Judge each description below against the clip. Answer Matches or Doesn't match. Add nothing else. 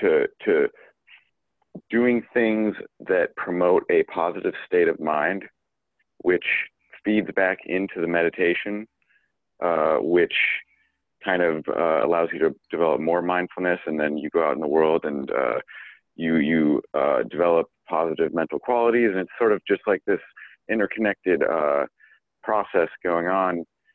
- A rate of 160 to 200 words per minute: Doesn't match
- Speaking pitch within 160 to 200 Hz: Doesn't match